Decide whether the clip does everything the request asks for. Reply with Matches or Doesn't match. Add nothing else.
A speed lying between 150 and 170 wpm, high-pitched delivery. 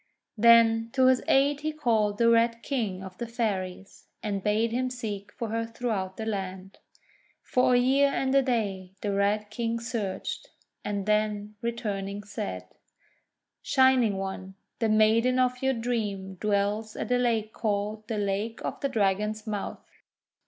Matches